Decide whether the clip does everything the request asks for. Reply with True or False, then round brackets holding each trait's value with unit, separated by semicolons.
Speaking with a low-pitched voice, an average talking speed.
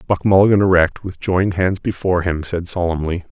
True (90 Hz; 175 wpm)